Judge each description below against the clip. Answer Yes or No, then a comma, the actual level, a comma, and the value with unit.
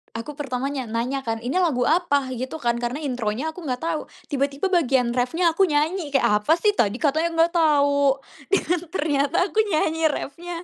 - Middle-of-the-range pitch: No, very high, 285 Hz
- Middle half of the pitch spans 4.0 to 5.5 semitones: Yes, average, 4.3 semitones